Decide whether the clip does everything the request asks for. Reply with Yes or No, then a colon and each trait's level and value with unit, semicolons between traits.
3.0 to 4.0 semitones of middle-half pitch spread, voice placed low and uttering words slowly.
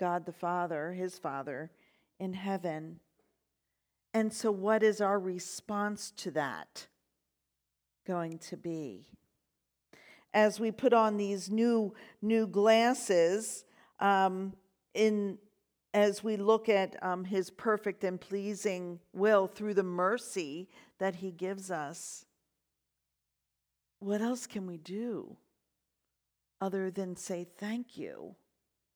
No: average, 3.5 semitones; high, 190 Hz; slow, 115 wpm